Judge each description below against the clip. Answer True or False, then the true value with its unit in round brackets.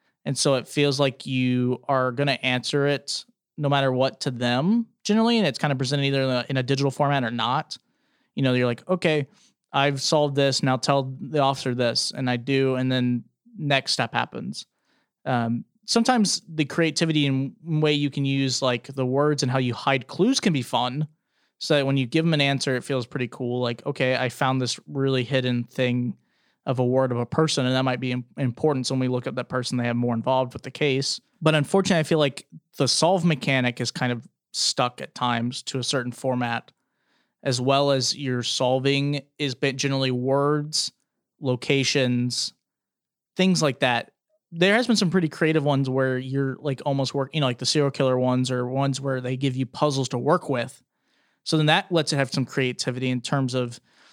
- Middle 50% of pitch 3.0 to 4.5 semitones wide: False (2.5 semitones)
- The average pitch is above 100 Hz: True (135 Hz)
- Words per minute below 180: False (205 wpm)